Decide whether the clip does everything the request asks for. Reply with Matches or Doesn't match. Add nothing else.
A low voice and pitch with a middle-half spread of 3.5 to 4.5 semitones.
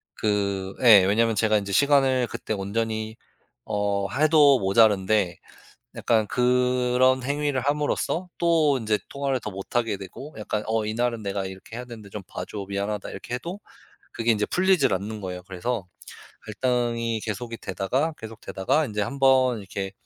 Matches